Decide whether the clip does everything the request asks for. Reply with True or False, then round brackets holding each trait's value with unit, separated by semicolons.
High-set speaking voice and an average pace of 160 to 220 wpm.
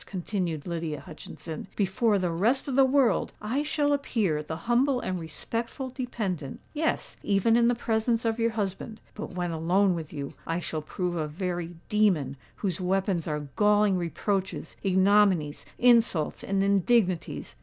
False (195 Hz; 150 wpm)